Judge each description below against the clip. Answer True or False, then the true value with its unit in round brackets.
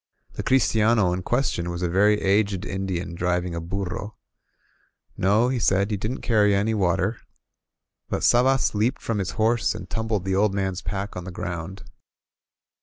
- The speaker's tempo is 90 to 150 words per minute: False (170 wpm)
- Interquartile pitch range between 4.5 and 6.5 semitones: False (3.2 semitones)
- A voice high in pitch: False (100 Hz)